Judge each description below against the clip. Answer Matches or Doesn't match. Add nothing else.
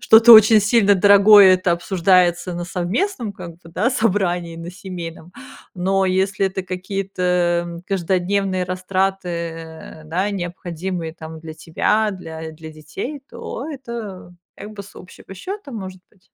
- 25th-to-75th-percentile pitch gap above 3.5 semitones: Doesn't match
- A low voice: Doesn't match